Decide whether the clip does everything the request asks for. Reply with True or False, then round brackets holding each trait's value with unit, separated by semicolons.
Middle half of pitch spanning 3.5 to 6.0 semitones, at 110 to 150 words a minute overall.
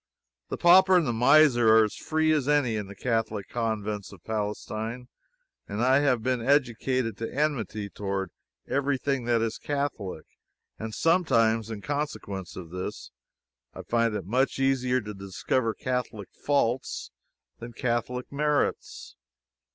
True (4.2 semitones; 140 wpm)